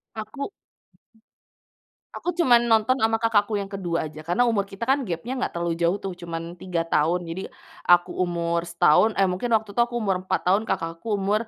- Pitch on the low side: No, high, 195 Hz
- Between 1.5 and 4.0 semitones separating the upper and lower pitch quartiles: No, average, 4.6 semitones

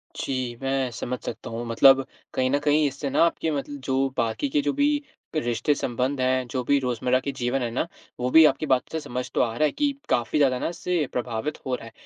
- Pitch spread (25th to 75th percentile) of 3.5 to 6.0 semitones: No, average, 2.7 semitones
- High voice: No, low, 135 Hz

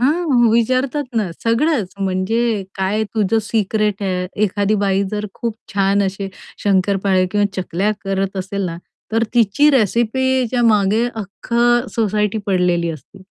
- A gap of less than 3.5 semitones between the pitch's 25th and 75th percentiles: Yes, average, 3.0 semitones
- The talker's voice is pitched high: Yes, high, 205 Hz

